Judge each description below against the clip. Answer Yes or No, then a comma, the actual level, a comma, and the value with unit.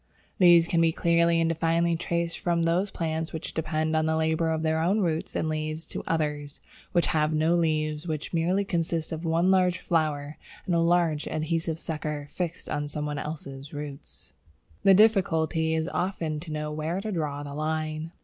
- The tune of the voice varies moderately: No, narrow, 1.6 semitones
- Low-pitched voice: No, medium, 160 Hz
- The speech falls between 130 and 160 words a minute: No, average, 190 wpm